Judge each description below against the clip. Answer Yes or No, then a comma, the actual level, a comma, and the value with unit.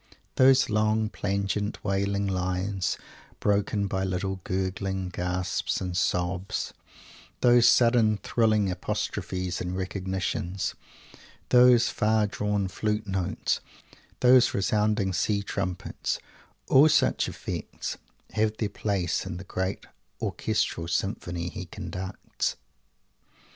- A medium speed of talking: No, slow, 100 wpm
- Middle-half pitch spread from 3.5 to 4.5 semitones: No, narrow, 2.5 semitones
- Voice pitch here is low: Yes, low, 100 Hz